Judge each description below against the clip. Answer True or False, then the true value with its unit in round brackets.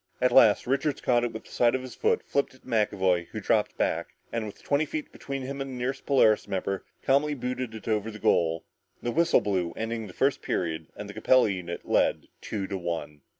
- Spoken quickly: True (225 wpm)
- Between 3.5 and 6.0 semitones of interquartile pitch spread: True (5.2 semitones)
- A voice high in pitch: False (115 Hz)